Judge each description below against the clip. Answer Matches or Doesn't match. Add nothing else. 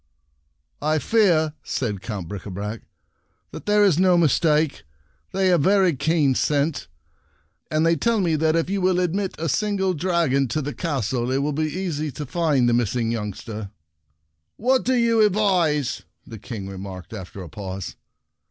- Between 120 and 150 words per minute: Doesn't match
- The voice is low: Doesn't match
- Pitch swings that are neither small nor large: Doesn't match